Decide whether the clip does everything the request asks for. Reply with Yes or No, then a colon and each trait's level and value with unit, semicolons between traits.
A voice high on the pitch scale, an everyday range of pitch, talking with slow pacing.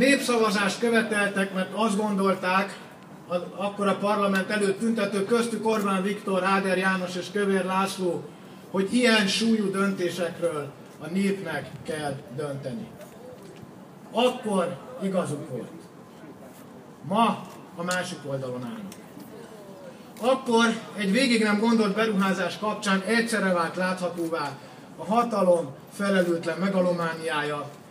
Yes: high, 195 Hz; average, 3.2 semitones; slow, 105 wpm